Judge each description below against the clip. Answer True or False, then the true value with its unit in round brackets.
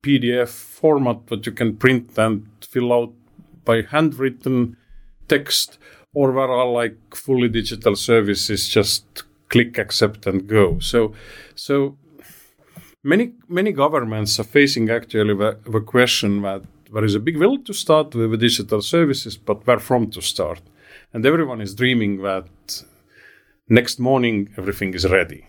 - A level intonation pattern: False (3.9 semitones)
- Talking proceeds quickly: False (145 wpm)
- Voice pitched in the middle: False (115 Hz)